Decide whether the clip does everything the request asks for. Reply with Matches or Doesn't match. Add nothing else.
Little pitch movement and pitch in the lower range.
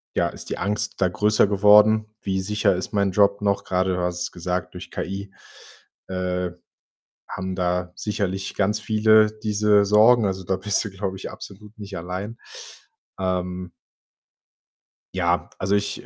Matches